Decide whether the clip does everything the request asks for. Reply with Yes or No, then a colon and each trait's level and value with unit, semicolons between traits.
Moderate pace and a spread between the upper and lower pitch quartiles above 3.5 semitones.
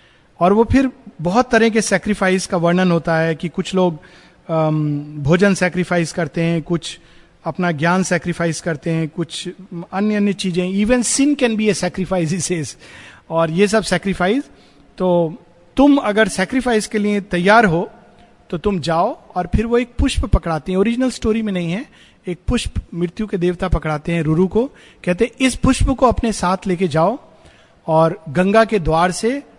Yes: average, 170 wpm; average, 4.1 semitones